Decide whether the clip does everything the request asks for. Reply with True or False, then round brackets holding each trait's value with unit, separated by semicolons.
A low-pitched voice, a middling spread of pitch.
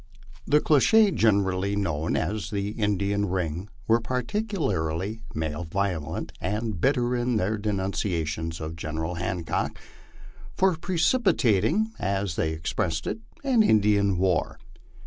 False (100 Hz; 5.8 semitones)